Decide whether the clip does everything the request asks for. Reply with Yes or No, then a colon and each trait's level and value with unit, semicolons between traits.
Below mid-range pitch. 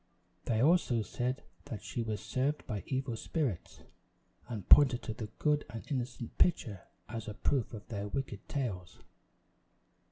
Yes: low, 120 Hz